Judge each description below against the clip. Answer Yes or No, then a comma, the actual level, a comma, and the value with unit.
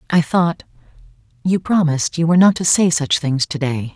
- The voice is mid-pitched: Yes, medium, 160 Hz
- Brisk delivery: No, average, 150 wpm